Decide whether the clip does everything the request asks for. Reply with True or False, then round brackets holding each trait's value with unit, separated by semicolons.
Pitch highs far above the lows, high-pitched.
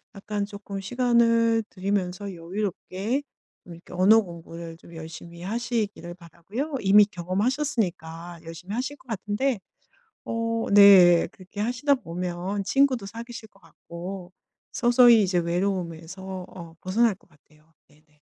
False (4.8 semitones; 195 Hz)